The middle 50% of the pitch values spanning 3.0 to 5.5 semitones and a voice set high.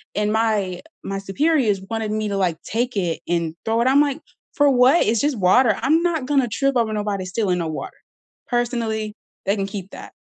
Yes: average, 4.5 semitones; high, 220 Hz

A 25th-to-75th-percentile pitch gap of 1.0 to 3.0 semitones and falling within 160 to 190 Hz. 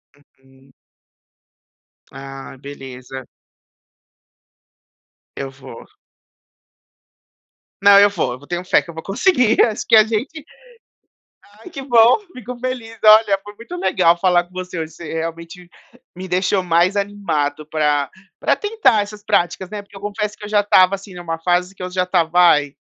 No: average, 4.5 semitones; medium, 185 Hz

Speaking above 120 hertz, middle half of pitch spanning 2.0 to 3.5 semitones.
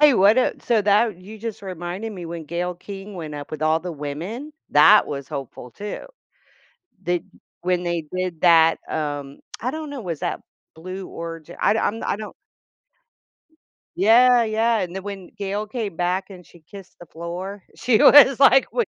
No: medium, 185 Hz; average, 4.5 semitones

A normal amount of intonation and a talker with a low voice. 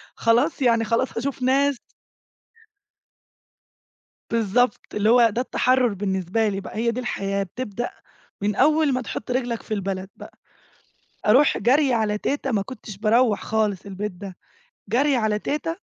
No: average, 3.7 semitones; high, 230 Hz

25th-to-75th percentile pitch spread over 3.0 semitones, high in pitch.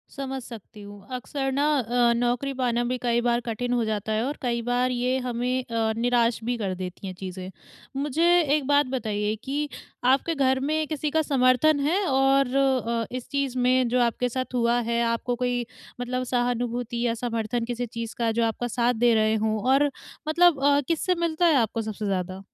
No: narrow, 2.6 semitones; high, 245 Hz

